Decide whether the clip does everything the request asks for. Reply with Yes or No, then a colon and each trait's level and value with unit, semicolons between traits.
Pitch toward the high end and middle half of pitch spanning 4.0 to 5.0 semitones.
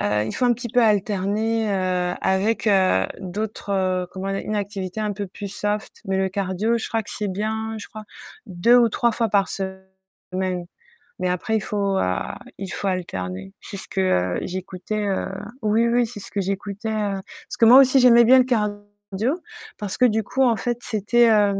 No: high, 205 Hz; average, 2.8 semitones